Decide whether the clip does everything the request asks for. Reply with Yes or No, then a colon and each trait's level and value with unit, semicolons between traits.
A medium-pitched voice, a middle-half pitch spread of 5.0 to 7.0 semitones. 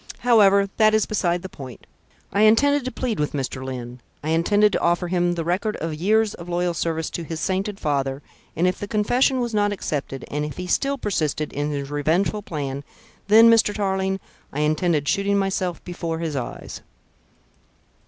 Yes: medium, 180 Hz; wide, 5.4 semitones